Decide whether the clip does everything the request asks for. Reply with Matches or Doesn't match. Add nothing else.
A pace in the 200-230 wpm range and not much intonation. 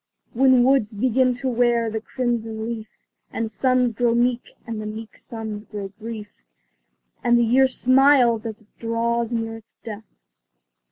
Doesn't match